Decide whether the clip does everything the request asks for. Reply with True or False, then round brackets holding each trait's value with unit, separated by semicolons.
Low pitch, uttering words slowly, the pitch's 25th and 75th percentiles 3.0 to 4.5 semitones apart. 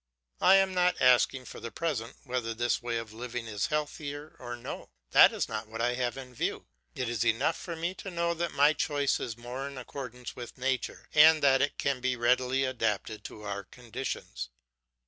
False (125 Hz; 205 wpm; 3.7 semitones)